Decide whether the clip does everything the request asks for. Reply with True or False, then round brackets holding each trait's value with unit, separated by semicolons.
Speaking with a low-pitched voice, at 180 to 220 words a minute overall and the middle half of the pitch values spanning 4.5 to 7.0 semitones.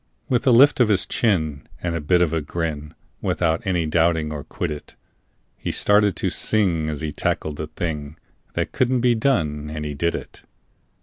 True (80 Hz; 185 wpm; 4.8 semitones)